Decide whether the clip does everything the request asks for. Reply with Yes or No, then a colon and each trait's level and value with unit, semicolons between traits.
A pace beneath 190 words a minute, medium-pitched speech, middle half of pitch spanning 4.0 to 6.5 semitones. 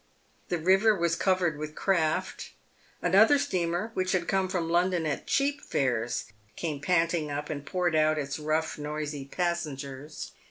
No: average, 150 wpm; medium, 165 Hz; average, 3.5 semitones